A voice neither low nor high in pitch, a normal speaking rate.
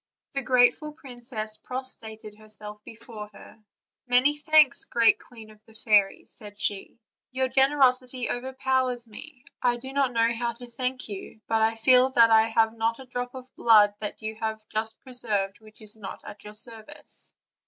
No: high, 230 Hz; average, 170 wpm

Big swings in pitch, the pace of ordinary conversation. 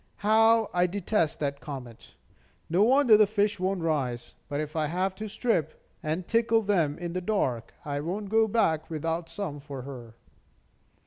Yes: wide, 6.0 semitones; average, 170 wpm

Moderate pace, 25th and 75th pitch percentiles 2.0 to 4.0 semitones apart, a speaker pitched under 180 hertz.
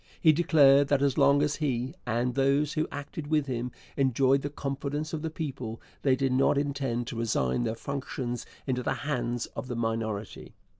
Yes: average, 185 wpm; average, 3.0 semitones; low, 135 Hz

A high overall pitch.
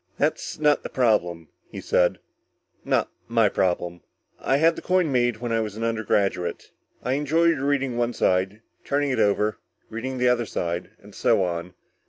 No: low, 115 Hz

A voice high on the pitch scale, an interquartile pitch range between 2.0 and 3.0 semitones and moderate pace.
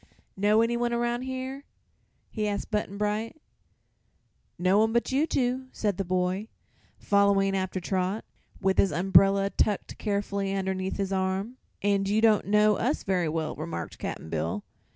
Yes: high, 200 Hz; average, 2.7 semitones; average, 150 wpm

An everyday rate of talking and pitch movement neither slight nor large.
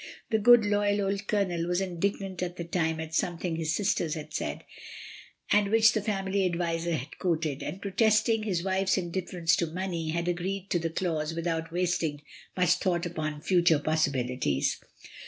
Yes: average, 165 wpm; average, 3.0 semitones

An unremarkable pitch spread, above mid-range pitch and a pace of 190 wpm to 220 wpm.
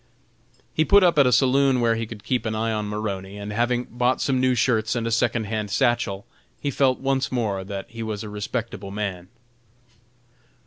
No: average, 3.5 semitones; low, 115 Hz; average, 195 wpm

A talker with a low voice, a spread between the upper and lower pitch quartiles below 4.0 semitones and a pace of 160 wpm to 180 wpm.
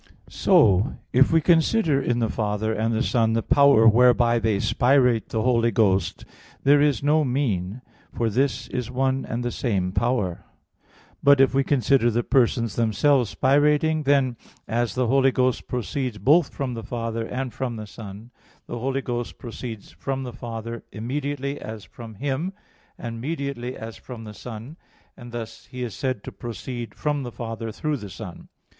Yes: low, 120 Hz; average, 3.2 semitones; average, 170 wpm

